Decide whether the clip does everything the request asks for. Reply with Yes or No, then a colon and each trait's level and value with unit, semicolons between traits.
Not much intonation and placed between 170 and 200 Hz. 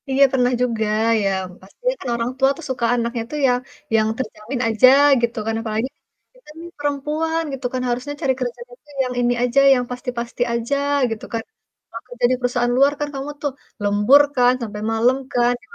No: narrow, 2.3 semitones; high, 245 Hz